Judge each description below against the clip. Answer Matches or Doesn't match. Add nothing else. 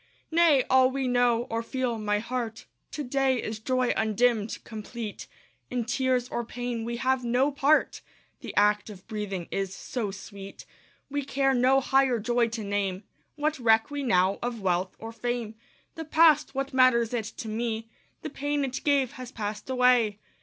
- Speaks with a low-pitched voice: Doesn't match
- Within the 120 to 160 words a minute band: Doesn't match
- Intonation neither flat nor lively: Matches